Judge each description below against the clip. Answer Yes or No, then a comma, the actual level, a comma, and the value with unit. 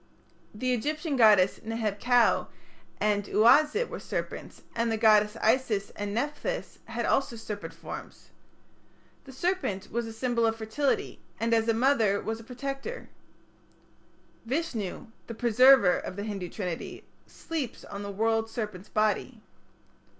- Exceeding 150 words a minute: No, slow, 135 wpm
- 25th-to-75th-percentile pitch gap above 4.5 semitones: No, average, 3.7 semitones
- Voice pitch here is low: No, high, 225 Hz